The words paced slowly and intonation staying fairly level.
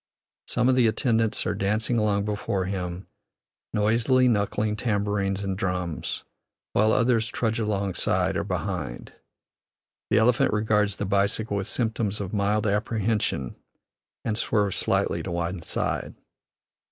Yes: slow, 130 wpm; narrow, 2.1 semitones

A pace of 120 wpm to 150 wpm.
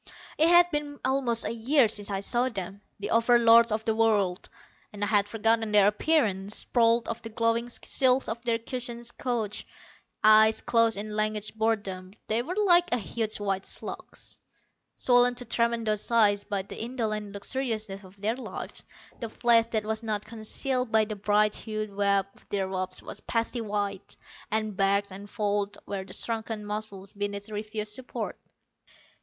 No: average, 165 wpm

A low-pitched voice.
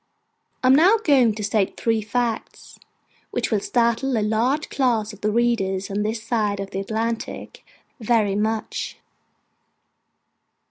No: high, 220 Hz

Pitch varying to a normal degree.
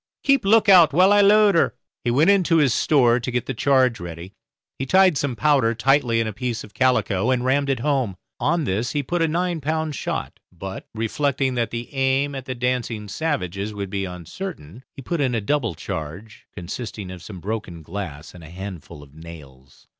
No: wide, 7.0 semitones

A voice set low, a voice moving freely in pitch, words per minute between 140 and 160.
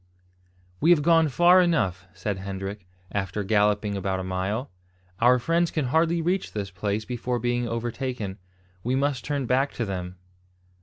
Yes: low, 120 Hz; wide, 6.4 semitones; average, 155 wpm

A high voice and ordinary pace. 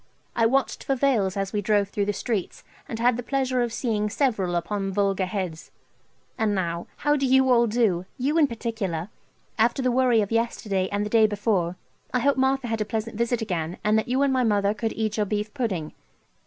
No: high, 220 Hz; fast, 210 wpm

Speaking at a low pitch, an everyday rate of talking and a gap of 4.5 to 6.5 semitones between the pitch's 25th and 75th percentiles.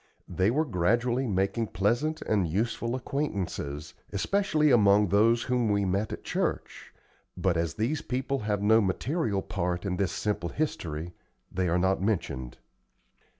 Yes: low, 105 Hz; average, 145 wpm; average, 4.8 semitones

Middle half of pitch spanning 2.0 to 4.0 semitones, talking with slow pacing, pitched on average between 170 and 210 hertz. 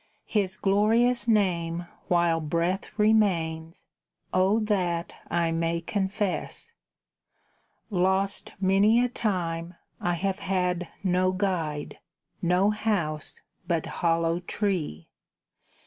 Yes: average, 3.2 semitones; slow, 95 wpm; medium, 185 Hz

